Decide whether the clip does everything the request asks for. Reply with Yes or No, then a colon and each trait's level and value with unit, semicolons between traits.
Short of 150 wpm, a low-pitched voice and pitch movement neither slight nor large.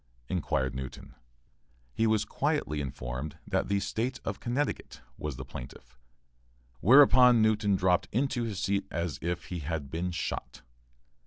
No: average, 140 wpm; very low, 90 Hz; wide, 6.8 semitones